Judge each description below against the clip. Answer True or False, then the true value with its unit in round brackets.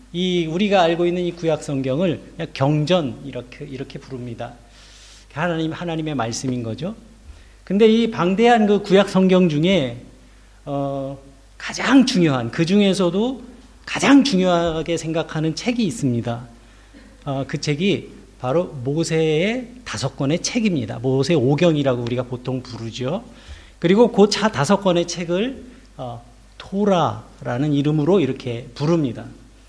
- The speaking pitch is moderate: True (155 Hz)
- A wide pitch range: True (6.5 semitones)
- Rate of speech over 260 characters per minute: True (275 characters per minute)